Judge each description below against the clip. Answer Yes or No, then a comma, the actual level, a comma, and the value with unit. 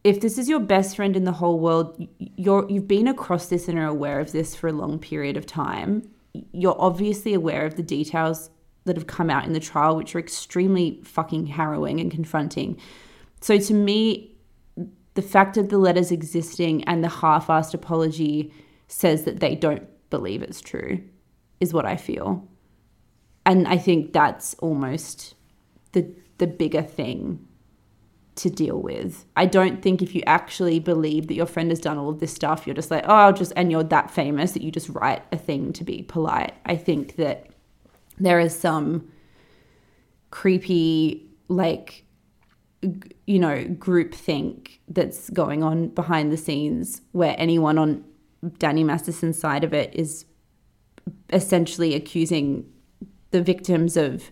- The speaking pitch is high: No, medium, 165 Hz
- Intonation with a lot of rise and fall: No, narrow, 2.6 semitones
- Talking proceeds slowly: No, average, 165 wpm